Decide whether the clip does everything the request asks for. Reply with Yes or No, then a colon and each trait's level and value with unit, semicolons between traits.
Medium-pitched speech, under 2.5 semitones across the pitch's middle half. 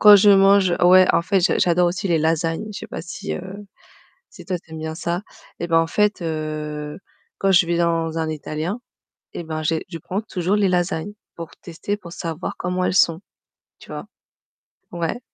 No: medium, 175 Hz; average, 2.8 semitones